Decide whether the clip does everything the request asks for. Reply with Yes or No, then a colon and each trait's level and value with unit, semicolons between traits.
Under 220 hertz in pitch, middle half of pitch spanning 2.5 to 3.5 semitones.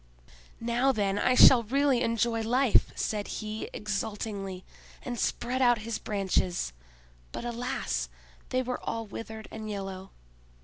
No: high, 225 Hz; average, 2.8 semitones